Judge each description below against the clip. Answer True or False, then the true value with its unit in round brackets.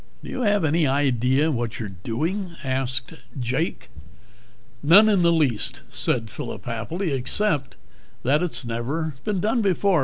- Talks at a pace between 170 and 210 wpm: False (145 wpm)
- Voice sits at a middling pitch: True (145 Hz)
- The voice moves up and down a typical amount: False (6.3 semitones)